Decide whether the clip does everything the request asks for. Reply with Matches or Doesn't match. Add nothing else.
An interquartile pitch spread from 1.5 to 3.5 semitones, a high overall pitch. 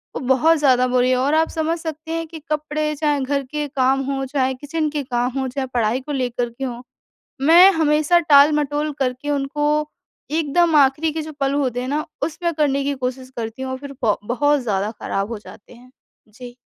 Matches